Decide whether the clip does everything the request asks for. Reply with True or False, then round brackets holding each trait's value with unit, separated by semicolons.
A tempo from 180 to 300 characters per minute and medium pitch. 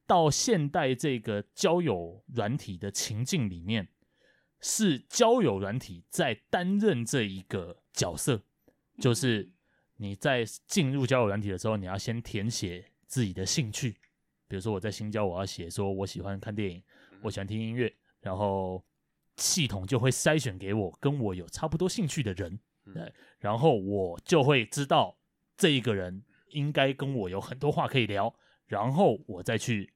False (240 characters per minute; 115 Hz)